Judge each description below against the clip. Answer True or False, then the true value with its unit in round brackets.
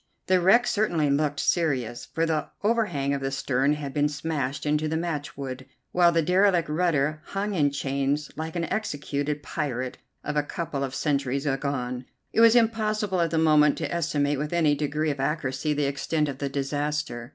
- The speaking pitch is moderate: True (150 Hz)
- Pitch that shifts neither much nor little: True (3.1 semitones)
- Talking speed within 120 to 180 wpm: True (175 wpm)